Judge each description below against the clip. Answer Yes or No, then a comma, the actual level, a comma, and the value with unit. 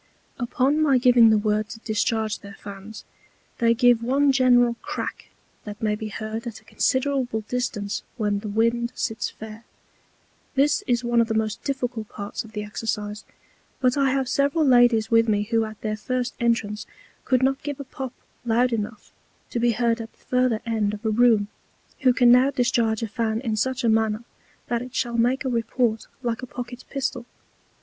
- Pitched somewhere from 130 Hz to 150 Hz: No, high, 235 Hz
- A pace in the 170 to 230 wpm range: Yes, average, 190 wpm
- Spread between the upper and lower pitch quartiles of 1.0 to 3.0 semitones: Yes, narrow, 2.5 semitones